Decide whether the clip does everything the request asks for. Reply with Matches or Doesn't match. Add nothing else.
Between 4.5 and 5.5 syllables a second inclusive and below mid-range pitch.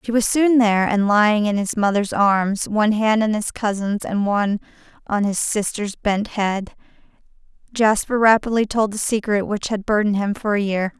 Doesn't match